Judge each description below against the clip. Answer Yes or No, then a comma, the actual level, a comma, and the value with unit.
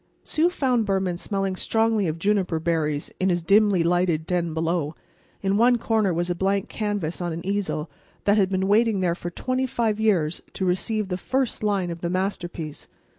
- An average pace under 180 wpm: No, average, 185 wpm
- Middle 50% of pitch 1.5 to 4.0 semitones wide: Yes, average, 3.5 semitones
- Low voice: No, high, 190 Hz